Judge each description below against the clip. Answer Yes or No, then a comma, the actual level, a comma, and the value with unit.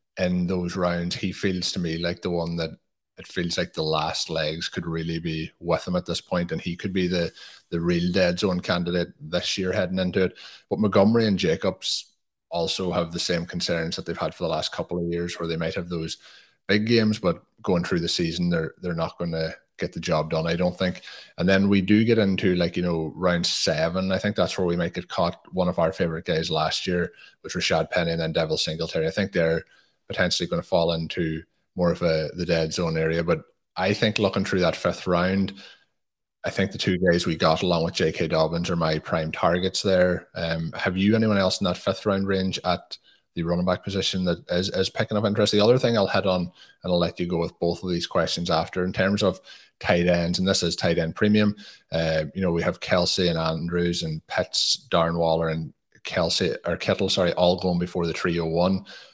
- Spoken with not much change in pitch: Yes, narrow, 2.3 semitones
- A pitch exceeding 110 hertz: No, very low, 90 Hz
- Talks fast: Yes, fast, 230 wpm